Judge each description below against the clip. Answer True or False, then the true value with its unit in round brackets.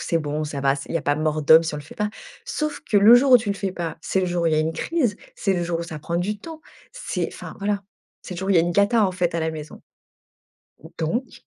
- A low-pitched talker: False (175 Hz)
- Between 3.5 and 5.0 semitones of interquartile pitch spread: True (4.5 semitones)